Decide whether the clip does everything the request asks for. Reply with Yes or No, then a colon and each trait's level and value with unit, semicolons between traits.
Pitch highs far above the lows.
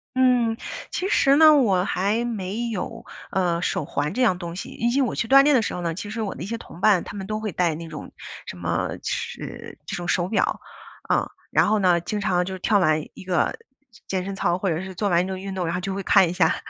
No: average, 4.1 semitones